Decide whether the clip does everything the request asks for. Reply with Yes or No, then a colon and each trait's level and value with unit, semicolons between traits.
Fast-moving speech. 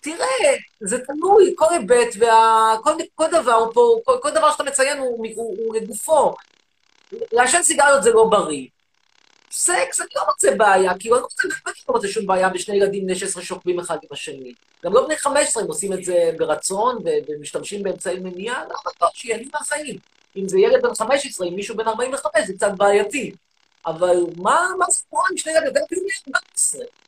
Yes: fast, 180 wpm